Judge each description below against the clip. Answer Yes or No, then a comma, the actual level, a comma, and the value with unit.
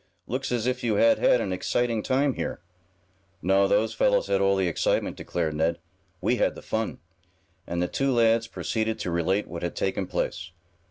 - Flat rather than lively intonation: No, average, 5.2 semitones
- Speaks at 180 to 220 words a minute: Yes, average, 185 wpm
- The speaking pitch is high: No, low, 110 Hz